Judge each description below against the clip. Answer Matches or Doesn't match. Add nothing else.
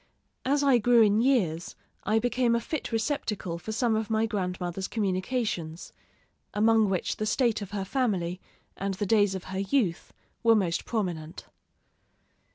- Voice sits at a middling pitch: Doesn't match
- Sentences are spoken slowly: Doesn't match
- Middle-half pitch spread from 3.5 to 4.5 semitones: Matches